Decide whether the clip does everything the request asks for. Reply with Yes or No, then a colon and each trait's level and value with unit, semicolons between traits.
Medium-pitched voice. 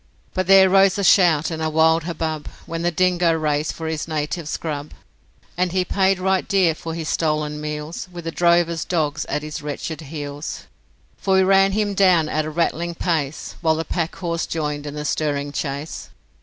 Yes: medium, 160 Hz